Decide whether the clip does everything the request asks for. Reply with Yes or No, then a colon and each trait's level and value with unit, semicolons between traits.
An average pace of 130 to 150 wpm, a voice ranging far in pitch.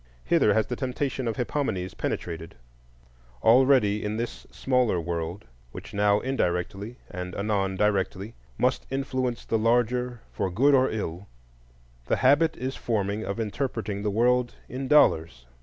No: average, 140 wpm; average, 4.5 semitones